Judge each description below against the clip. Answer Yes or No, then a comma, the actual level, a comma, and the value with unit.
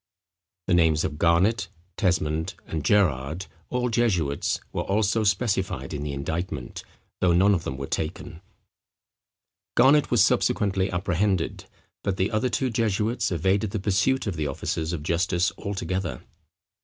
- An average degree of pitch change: Yes, average, 4.3 semitones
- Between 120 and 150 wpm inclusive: Yes, average, 140 wpm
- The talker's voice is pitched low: Yes, very low, 95 Hz